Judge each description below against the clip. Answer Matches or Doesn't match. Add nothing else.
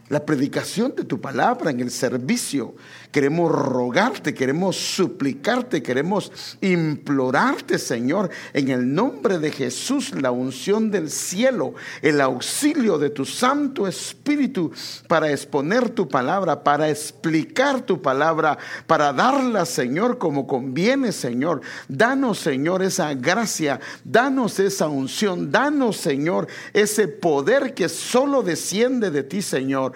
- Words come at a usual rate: Doesn't match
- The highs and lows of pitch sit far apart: Matches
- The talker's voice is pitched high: Doesn't match